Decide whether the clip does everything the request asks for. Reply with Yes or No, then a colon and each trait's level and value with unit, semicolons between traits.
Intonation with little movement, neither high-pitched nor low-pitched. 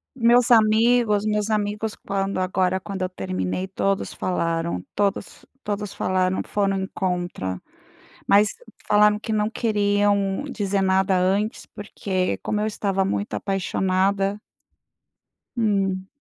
No: narrow, 1.9 semitones; high, 200 Hz